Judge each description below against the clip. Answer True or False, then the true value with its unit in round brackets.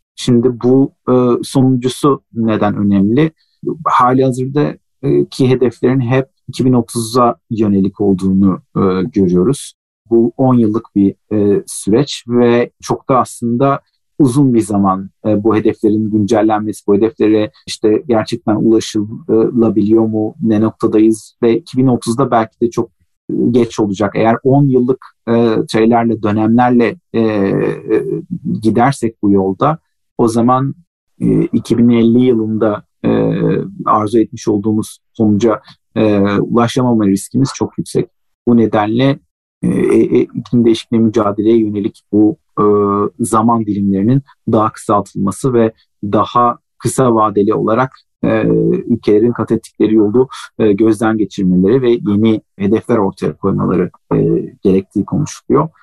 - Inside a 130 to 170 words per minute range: False (110 wpm)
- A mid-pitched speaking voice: False (110 Hz)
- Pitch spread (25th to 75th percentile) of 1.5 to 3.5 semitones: True (2.5 semitones)